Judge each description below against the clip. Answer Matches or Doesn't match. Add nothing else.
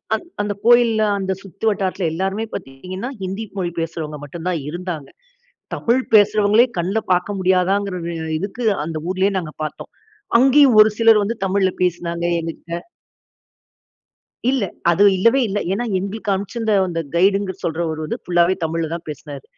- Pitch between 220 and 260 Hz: Doesn't match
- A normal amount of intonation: Matches